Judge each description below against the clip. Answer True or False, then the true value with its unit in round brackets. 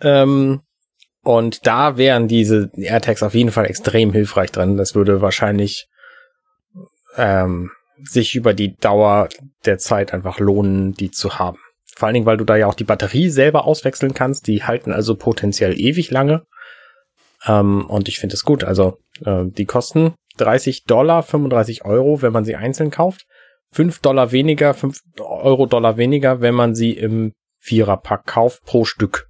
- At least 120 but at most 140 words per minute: False (160 wpm)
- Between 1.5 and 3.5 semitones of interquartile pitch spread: False (5.0 semitones)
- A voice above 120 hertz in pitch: False (115 Hz)